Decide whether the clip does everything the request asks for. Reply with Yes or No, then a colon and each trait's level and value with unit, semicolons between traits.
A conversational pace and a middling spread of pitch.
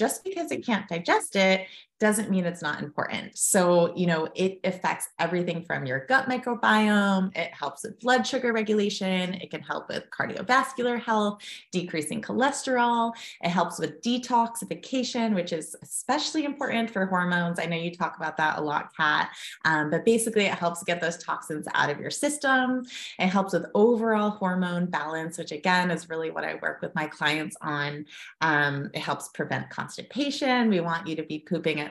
No: average, 180 wpm; wide, 5.9 semitones